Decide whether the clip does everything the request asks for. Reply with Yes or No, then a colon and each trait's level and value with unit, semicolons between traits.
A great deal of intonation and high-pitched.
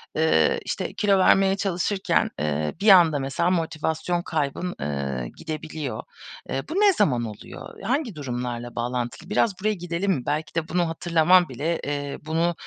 No: wide, 5.9 semitones; medium, 160 Hz